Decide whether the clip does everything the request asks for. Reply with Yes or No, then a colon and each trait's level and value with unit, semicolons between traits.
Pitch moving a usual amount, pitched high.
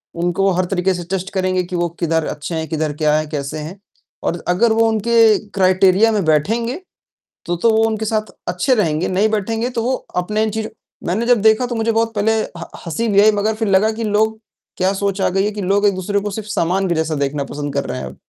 Yes: average, 4.0 semitones; high, 195 Hz